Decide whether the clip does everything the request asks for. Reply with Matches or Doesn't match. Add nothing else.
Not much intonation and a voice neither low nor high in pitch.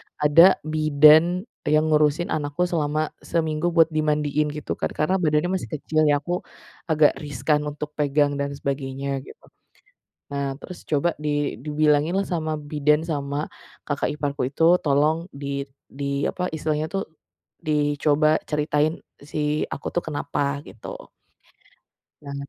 Matches